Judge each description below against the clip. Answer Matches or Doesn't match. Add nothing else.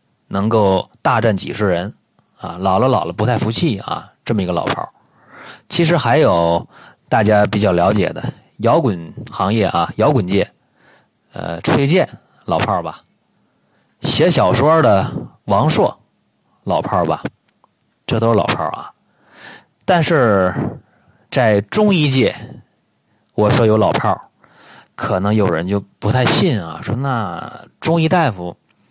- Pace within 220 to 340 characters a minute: Doesn't match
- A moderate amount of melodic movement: Doesn't match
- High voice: Doesn't match